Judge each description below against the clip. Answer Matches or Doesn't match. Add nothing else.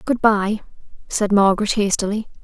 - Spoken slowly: Matches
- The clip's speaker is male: Doesn't match